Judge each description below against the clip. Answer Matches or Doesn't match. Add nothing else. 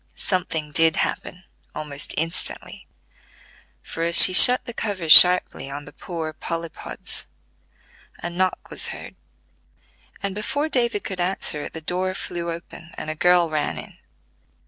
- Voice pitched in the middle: Matches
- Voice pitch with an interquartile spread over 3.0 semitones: Doesn't match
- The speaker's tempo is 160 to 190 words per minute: Doesn't match